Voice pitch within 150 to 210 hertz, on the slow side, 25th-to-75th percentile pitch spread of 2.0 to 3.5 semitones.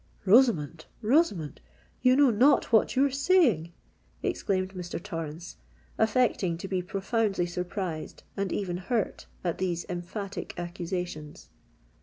No: high, 190 Hz; slow, 110 wpm; average, 4.6 semitones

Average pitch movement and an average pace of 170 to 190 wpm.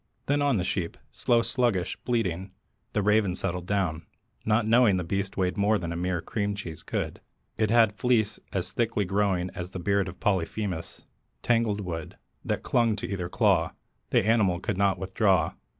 Yes: average, 3.3 semitones; average, 175 wpm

